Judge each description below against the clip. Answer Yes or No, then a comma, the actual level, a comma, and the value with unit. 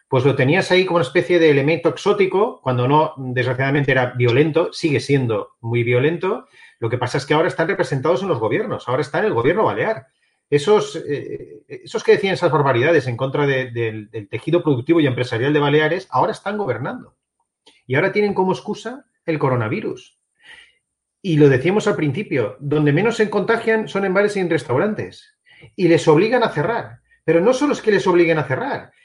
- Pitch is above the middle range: No, medium, 160 Hz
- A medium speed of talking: No, fast, 195 wpm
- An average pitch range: No, wide, 6.5 semitones